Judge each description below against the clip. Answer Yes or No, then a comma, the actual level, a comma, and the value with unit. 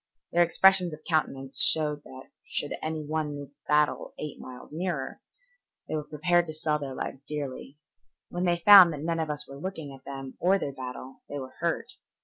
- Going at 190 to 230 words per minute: Yes, average, 195 wpm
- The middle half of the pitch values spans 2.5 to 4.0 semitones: Yes, average, 3.5 semitones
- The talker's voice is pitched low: No, medium, 150 Hz